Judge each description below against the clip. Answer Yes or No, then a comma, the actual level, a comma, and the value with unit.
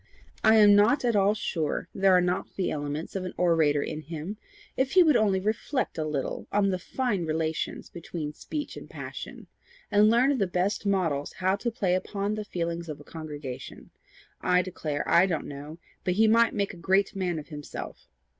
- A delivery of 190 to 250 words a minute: Yes, average, 195 wpm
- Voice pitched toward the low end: No, medium, 185 Hz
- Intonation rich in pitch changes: No, average, 4.6 semitones